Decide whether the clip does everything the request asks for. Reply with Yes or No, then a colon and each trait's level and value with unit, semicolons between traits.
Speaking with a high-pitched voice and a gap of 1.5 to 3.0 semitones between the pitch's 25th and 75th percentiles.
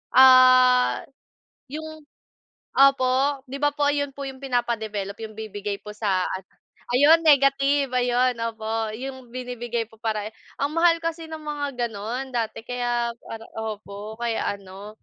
No: very high, 250 Hz; average, 3.9 semitones